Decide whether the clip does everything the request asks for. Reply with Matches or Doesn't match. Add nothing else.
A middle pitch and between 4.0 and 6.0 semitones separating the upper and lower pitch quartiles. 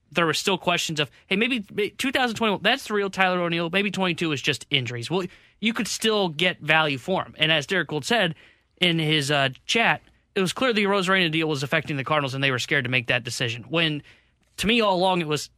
Matches